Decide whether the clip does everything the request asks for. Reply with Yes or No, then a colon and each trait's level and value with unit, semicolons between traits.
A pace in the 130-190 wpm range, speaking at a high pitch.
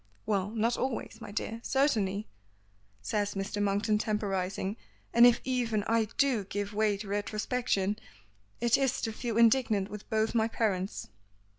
Yes: average, 150 wpm; high, 215 Hz